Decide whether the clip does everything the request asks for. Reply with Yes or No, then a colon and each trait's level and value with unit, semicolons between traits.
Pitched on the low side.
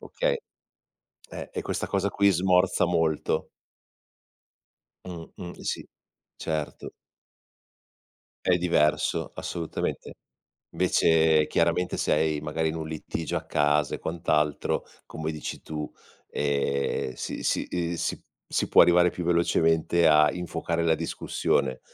Yes: very low, 80 Hz